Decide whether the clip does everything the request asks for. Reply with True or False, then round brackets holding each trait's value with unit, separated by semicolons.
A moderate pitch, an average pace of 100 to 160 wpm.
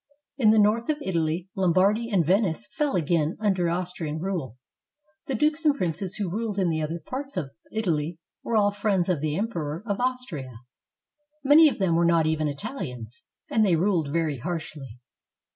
False (180 Hz; 175 wpm)